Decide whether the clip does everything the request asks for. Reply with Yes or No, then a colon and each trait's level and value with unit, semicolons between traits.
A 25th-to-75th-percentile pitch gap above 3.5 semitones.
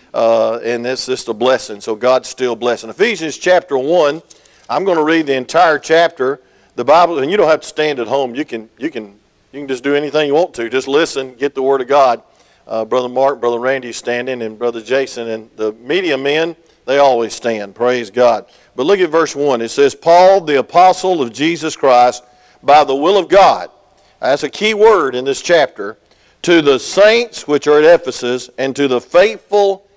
Yes: average, 4.5 semitones